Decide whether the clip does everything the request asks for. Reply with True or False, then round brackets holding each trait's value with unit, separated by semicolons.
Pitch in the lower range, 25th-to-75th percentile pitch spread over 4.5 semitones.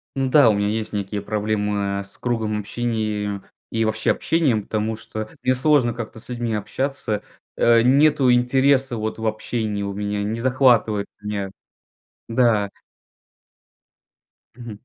False (110 Hz; 2.9 semitones)